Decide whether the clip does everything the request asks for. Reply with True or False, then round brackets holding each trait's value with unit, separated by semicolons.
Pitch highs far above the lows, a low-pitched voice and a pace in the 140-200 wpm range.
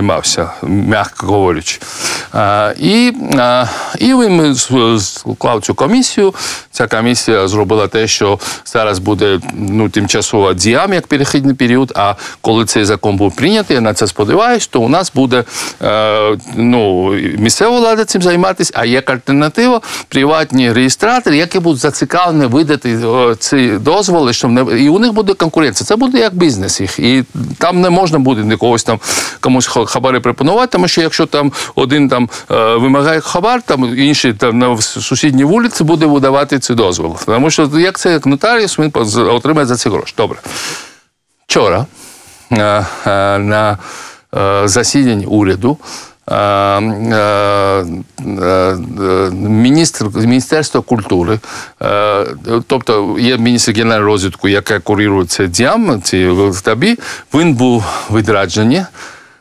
False (6.5 semitones; 125 Hz; 125 wpm)